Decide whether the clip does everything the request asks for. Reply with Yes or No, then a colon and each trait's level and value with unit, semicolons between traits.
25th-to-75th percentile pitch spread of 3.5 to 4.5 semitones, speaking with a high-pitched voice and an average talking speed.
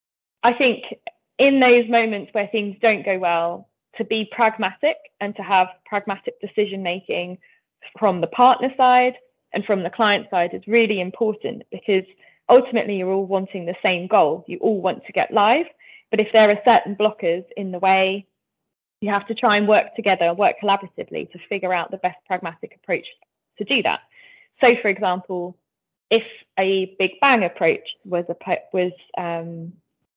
Yes: average, 3.8 semitones; high, 205 Hz; average, 165 wpm